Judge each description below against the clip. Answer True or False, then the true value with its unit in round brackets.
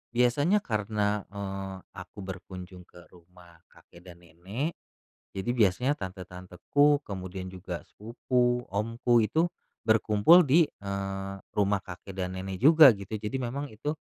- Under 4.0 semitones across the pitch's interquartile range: False (4.7 semitones)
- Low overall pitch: True (100 Hz)